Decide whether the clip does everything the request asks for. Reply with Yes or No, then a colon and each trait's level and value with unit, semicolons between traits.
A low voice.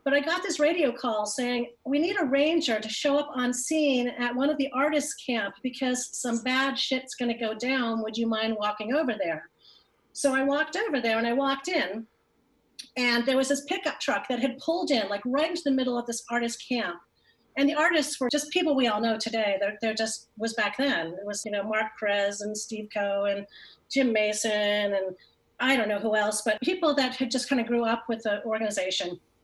No: high, 245 Hz